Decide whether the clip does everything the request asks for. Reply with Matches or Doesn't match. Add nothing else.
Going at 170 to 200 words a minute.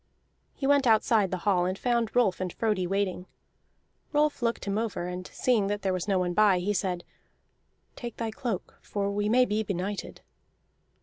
Matches